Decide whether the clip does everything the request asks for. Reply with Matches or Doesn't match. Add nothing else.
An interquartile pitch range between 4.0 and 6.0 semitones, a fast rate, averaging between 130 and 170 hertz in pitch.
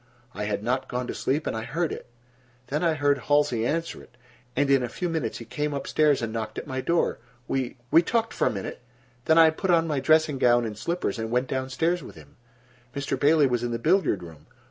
Matches